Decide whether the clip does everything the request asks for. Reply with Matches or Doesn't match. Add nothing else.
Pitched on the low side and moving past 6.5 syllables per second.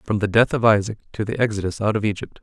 Matches